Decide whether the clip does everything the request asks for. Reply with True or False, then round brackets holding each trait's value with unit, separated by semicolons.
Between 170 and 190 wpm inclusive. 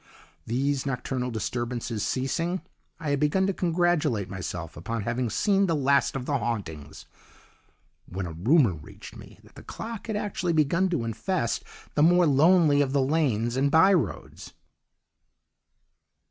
False (145 wpm)